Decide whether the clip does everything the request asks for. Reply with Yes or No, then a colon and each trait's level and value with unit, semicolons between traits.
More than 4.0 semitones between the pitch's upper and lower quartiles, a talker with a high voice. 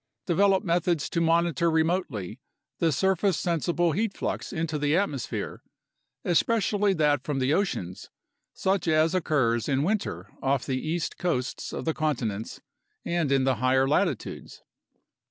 No: average, 4.8 semitones; medium, 160 Hz